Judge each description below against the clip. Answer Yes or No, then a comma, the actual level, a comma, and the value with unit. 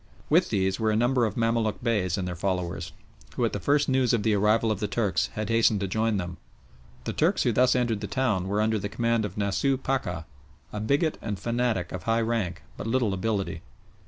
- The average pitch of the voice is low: Yes, low, 110 Hz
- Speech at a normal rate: No, fast, 215 wpm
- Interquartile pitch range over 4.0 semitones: No, average, 3.3 semitones